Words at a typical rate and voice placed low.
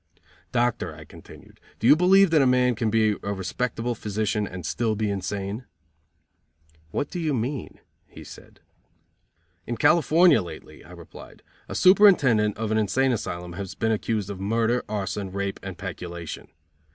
Yes: average, 155 wpm; low, 110 Hz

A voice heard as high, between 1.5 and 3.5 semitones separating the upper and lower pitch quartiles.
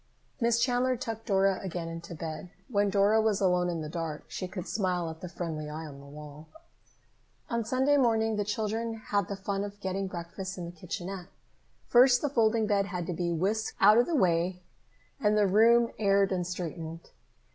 No: high, 195 Hz; average, 4.3 semitones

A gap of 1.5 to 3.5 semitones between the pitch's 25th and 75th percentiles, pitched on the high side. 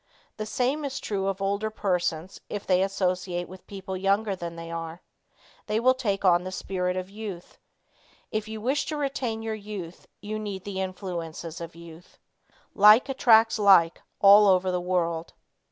Yes: average, 3.2 semitones; high, 195 Hz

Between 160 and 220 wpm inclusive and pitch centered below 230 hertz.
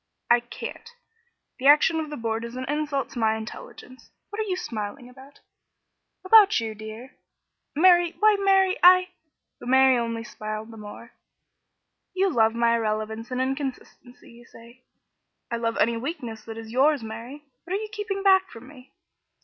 No: average, 175 wpm; very high, 255 Hz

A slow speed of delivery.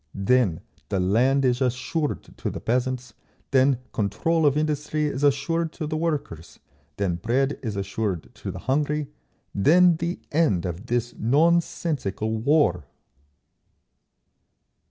Yes: slow, 125 wpm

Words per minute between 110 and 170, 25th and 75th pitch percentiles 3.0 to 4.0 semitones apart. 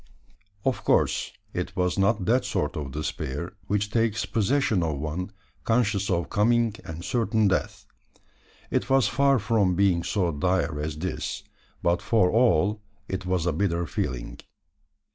No: average, 145 wpm; average, 4.7 semitones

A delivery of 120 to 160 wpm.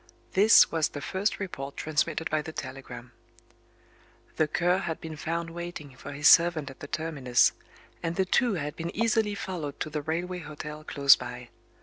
No: average, 170 wpm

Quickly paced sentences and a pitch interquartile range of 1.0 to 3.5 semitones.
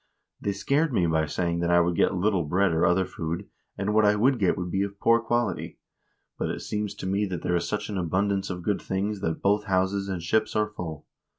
Yes: fast, 235 wpm; average, 3.2 semitones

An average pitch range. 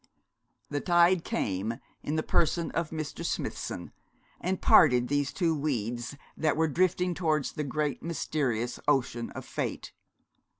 Yes: average, 4.9 semitones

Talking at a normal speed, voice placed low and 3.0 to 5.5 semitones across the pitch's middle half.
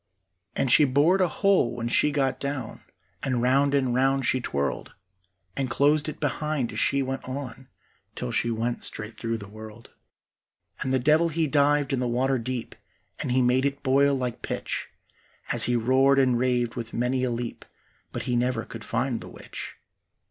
No: average, 185 wpm; low, 130 Hz; narrow, 2.5 semitones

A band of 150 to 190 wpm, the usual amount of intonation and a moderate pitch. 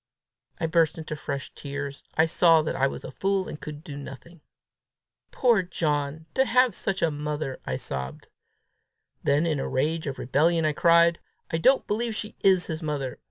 Yes: average, 180 wpm; average, 3.3 semitones; medium, 160 Hz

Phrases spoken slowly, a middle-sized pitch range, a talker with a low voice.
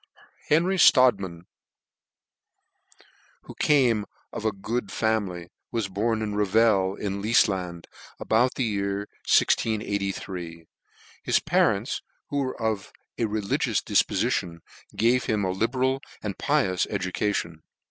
Yes: slow, 115 wpm; average, 3.4 semitones; low, 105 Hz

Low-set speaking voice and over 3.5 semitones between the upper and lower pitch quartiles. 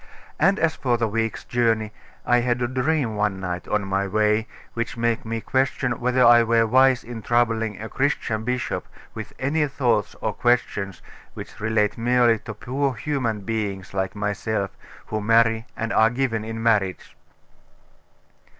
No: low, 115 Hz; narrow, 2.5 semitones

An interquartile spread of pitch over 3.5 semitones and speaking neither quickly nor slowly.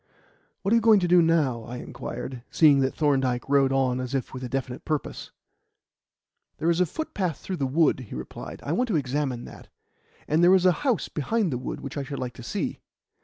No: average, 5.2 semitones; fast, 220 wpm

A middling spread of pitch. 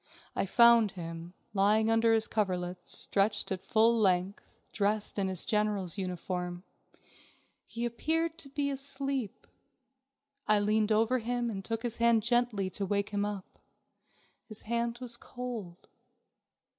Yes: average, 3.3 semitones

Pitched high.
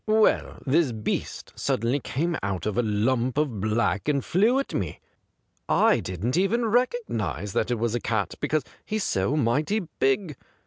No: low, 130 Hz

